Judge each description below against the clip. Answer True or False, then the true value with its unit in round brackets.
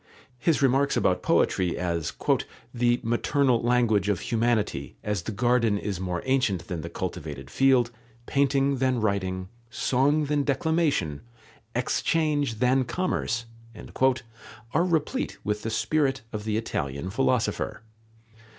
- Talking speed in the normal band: False (125 wpm)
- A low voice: True (120 Hz)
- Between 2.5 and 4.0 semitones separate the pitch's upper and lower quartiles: False (5.2 semitones)